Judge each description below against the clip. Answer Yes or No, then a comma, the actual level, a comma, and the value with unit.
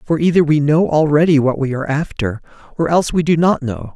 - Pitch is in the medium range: Yes, medium, 150 Hz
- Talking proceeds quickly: Yes, fast, 230 wpm